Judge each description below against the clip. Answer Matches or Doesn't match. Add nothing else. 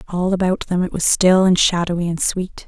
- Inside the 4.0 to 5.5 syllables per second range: Matches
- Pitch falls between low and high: Matches